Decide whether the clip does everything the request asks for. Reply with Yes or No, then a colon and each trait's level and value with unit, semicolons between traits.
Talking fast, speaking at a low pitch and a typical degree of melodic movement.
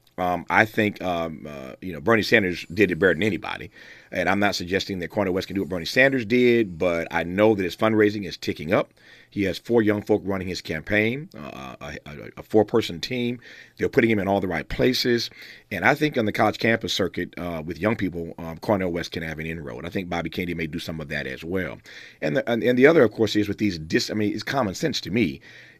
Yes: fast, 250 wpm; low, 100 Hz; average, 4.4 semitones